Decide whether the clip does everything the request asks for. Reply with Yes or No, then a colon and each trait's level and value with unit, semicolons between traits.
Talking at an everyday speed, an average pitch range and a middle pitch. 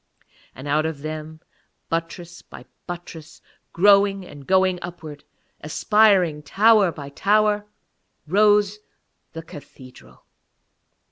No: slow, 95 wpm; average, 4.6 semitones; medium, 175 Hz